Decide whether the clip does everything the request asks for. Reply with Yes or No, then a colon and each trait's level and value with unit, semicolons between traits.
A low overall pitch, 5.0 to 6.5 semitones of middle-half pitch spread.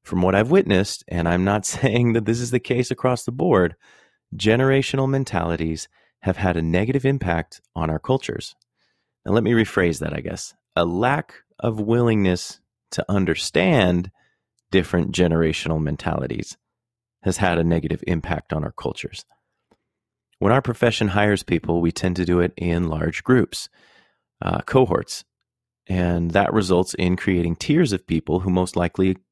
Yes: very low, 95 Hz; wide, 5.5 semitones